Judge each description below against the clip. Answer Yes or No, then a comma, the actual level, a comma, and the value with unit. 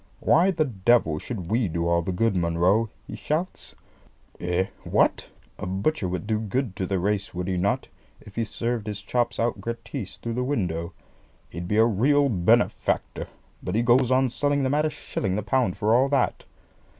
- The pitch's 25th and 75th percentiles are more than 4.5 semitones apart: Yes, wide, 5.6 semitones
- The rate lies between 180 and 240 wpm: Yes, average, 190 wpm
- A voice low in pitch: Yes, low, 110 Hz